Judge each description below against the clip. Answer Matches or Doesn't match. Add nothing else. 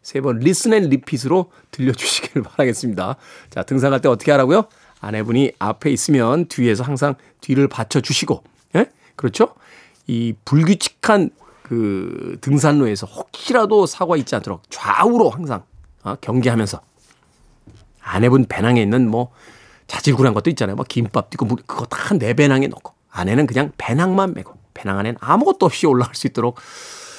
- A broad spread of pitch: Doesn't match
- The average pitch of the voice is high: Doesn't match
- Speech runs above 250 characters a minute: Matches